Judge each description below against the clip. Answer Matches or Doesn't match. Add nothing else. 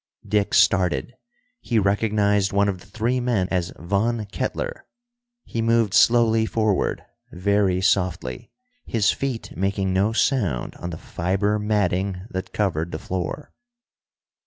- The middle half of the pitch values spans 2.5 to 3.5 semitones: Matches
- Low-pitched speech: Matches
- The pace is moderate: Doesn't match